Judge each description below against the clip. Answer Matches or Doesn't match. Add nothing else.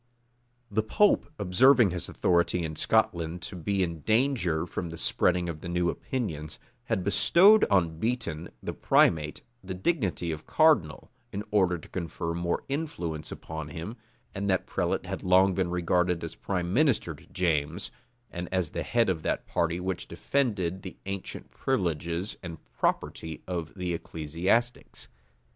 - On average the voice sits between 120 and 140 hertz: Doesn't match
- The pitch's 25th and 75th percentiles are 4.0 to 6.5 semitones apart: Doesn't match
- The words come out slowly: Doesn't match